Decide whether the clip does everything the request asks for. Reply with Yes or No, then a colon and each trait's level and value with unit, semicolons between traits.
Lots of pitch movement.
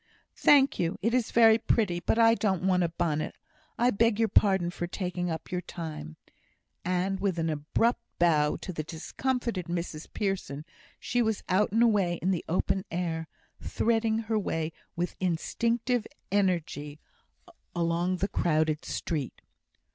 No: average, 4.9 semitones